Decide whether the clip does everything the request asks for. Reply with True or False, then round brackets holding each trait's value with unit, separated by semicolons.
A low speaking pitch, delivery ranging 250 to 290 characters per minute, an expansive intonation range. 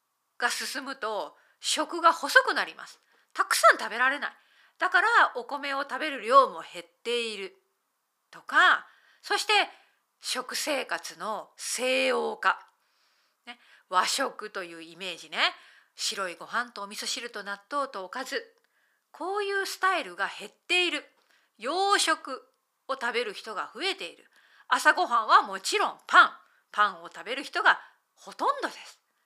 False (265 Hz; 275 characters per minute; 8.3 semitones)